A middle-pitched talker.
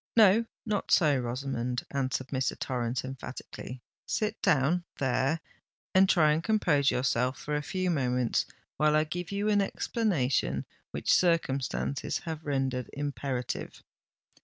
Yes: medium, 145 Hz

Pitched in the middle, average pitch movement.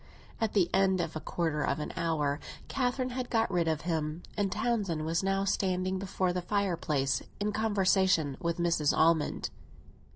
Yes: medium, 180 Hz; average, 3.7 semitones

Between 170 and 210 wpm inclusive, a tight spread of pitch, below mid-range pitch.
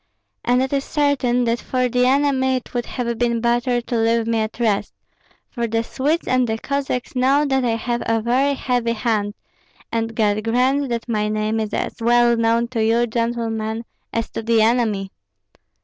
No: average, 185 wpm; narrow, 1.9 semitones; high, 235 Hz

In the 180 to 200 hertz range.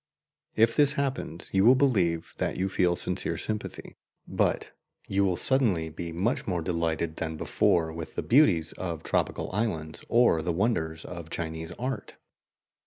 No: very low, 90 Hz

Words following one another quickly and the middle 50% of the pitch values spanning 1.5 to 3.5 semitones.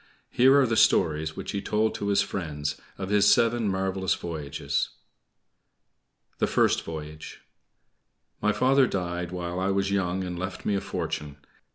No: average, 155 wpm; average, 3.0 semitones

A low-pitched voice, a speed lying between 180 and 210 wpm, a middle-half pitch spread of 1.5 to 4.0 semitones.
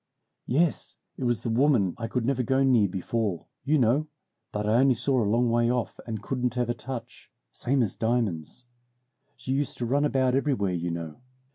Yes: low, 120 Hz; average, 185 wpm; average, 3.1 semitones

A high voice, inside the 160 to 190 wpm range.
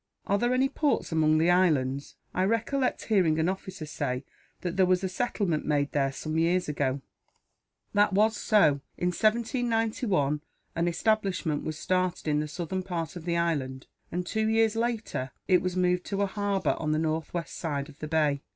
No: medium, 180 Hz; average, 180 wpm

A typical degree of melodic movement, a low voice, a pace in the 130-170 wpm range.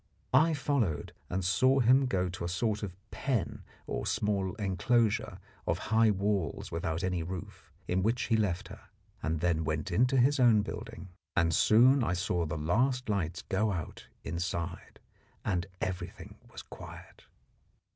Yes: average, 5.0 semitones; very low, 95 Hz; average, 160 wpm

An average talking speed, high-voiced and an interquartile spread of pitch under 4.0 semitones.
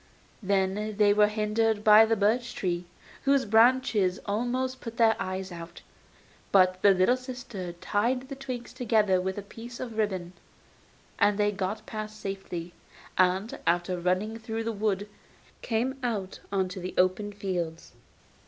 Yes: average, 150 wpm; high, 210 Hz; average, 3.4 semitones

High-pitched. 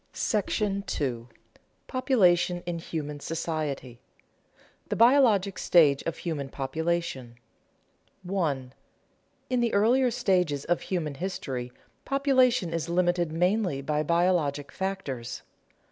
No: medium, 170 Hz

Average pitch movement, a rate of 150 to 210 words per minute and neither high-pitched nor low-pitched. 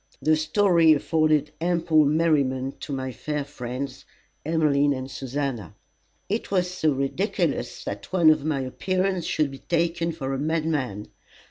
No: average, 3.5 semitones; average, 140 wpm; medium, 155 Hz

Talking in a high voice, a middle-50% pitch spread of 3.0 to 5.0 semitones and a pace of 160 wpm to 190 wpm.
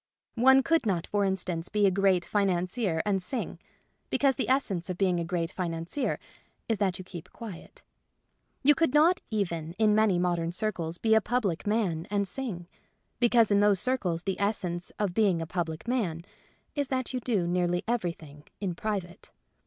Yes: high, 195 Hz; average, 4.4 semitones; average, 175 wpm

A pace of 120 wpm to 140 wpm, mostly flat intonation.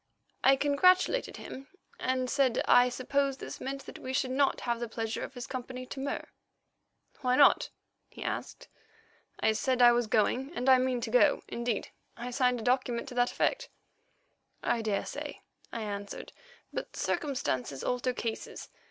No: average, 160 wpm; narrow, 2.1 semitones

